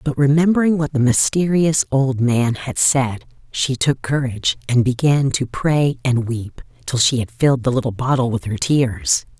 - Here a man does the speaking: No, female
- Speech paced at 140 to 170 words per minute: No, average, 180 wpm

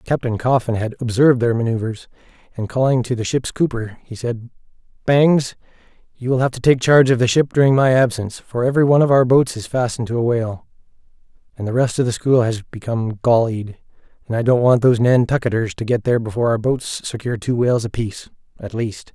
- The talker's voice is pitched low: Yes, low, 120 Hz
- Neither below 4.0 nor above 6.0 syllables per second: No, 6.3 syllables/s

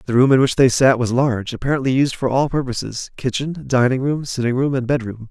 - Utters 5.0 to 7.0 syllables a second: Yes, 5.9 syllables/s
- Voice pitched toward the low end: Yes, low, 130 Hz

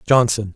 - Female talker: No, male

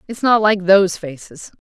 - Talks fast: No, average, 185 wpm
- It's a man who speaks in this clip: No, female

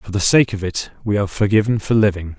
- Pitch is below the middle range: Yes, low, 100 Hz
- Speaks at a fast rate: Yes, fast, 250 wpm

